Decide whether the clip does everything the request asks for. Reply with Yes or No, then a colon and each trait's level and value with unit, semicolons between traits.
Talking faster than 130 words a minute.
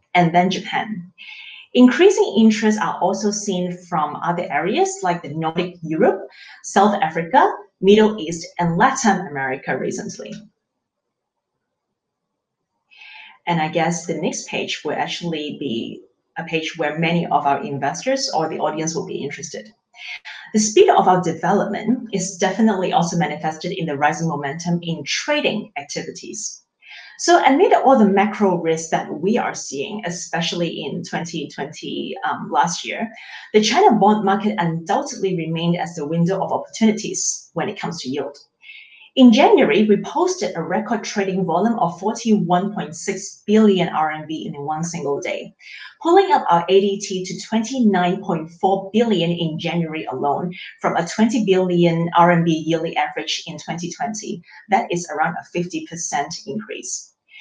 Yes: average, 140 wpm